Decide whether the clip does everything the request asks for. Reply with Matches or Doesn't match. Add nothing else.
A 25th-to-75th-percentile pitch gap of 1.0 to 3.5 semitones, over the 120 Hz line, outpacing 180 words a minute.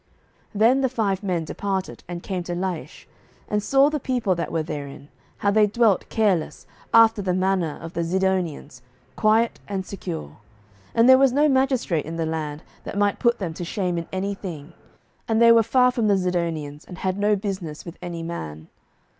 Doesn't match